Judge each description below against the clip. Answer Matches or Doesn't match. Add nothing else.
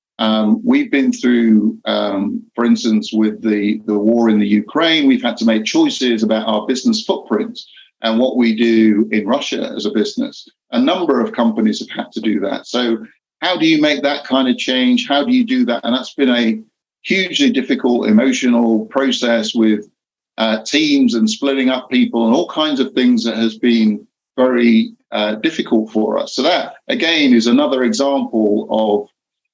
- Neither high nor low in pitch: Doesn't match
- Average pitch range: Matches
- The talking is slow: Doesn't match